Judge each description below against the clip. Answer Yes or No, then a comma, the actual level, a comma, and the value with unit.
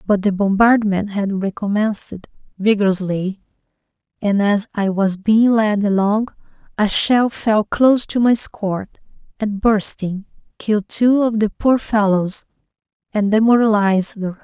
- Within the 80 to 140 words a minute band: Yes, slow, 135 wpm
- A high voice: Yes, high, 210 Hz